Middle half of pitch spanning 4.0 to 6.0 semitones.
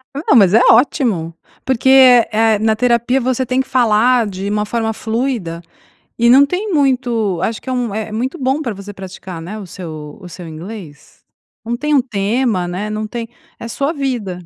Yes: average, 4.7 semitones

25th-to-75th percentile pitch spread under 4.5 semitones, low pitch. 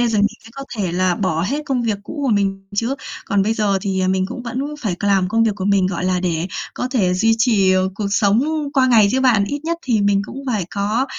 No: average, 3.9 semitones; high, 205 Hz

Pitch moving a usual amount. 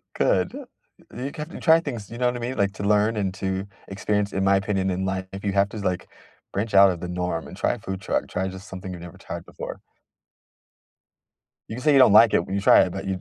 No: narrow, 2.3 semitones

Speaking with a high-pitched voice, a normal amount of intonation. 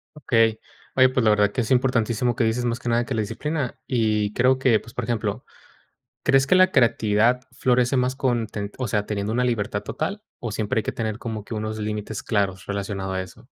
No: low, 115 Hz; average, 3.0 semitones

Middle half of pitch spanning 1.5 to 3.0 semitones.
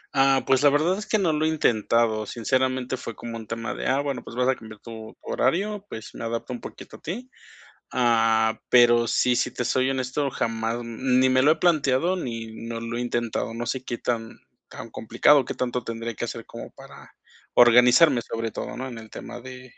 Yes: average, 2.7 semitones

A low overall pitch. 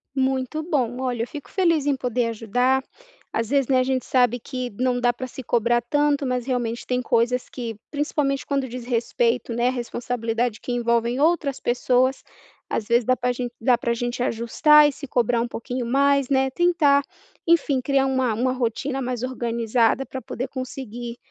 No: very high, 250 Hz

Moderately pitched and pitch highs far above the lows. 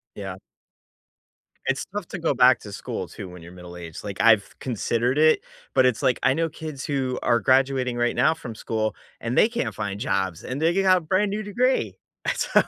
No: low, 130 Hz; wide, 7.0 semitones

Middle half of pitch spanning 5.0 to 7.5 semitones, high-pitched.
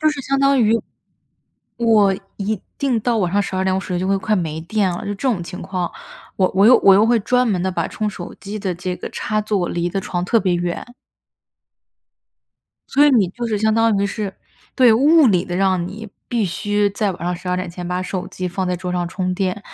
No: average, 3.3 semitones; high, 195 Hz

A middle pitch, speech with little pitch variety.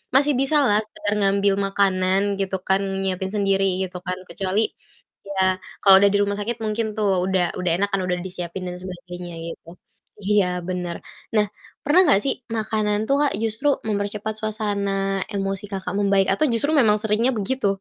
No: high, 200 Hz; narrow, 2.2 semitones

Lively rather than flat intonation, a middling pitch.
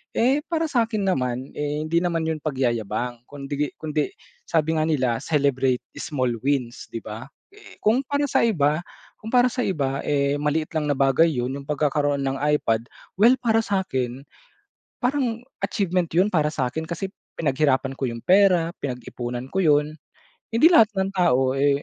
Yes: wide, 5.9 semitones; medium, 150 Hz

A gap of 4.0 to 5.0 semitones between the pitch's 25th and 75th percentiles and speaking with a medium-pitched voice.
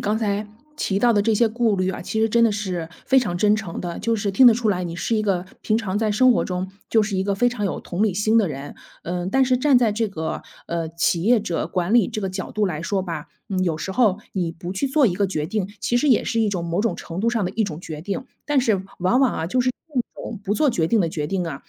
No: average, 4.3 semitones; high, 205 Hz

